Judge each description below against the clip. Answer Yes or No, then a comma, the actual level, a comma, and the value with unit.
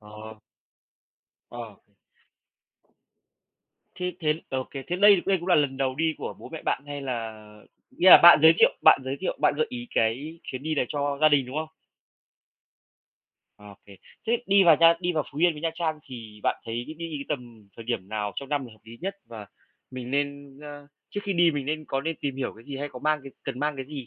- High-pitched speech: No, medium, 140 Hz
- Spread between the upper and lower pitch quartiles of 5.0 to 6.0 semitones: No, average, 4.5 semitones